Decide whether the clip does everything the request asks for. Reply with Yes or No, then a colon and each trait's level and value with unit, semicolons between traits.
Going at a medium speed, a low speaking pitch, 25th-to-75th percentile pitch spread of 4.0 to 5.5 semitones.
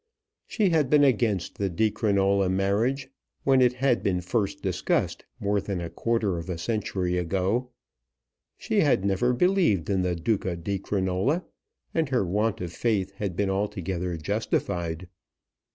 Yes: average, 150 wpm; low, 100 Hz; average, 4.3 semitones